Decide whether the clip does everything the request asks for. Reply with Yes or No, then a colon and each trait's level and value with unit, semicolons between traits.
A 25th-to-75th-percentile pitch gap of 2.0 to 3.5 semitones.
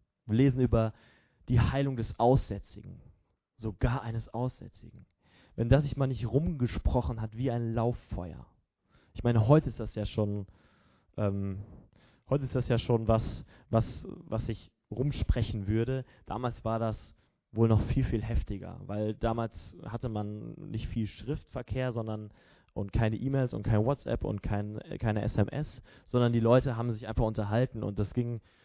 Yes: average, 2.9 semitones